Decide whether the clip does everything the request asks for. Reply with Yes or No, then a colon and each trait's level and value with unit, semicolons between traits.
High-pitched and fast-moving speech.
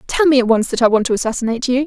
Yes: high, 245 Hz; fast, 320 wpm